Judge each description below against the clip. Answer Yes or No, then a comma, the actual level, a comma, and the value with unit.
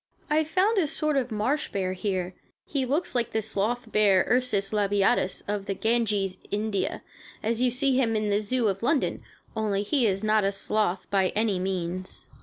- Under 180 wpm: No, average, 185 wpm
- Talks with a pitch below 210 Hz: No, high, 215 Hz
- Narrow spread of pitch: No, average, 4.1 semitones